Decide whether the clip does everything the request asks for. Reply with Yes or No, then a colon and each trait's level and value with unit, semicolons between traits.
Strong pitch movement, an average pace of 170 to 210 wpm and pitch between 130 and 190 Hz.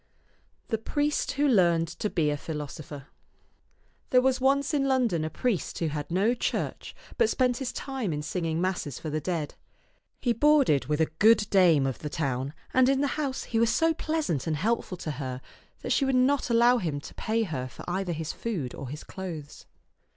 Yes: wide, 8.8 semitones; average, 195 wpm; medium, 185 Hz